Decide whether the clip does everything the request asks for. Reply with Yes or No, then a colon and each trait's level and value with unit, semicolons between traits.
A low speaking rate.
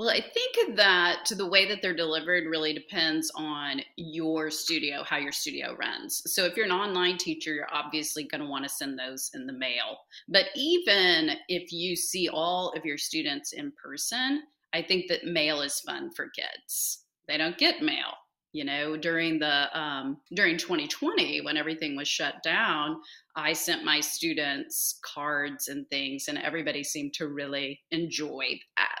No: average, 175 wpm